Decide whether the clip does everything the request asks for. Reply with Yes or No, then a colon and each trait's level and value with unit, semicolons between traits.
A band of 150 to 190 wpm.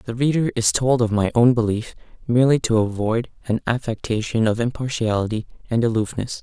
Yes: average, 160 wpm